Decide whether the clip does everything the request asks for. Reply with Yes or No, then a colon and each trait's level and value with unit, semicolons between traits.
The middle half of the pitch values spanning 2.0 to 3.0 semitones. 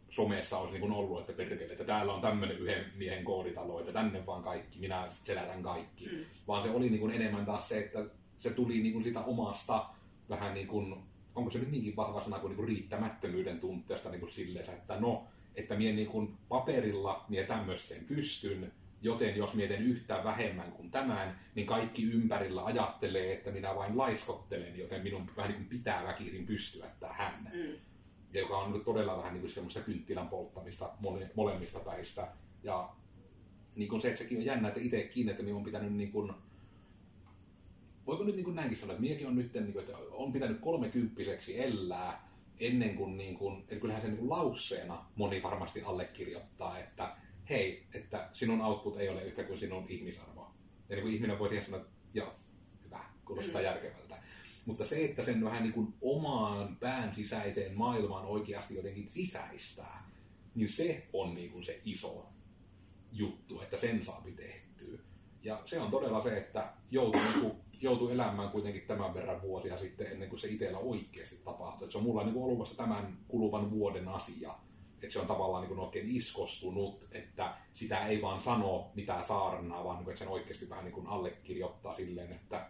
Yes: narrow, 2.4 semitones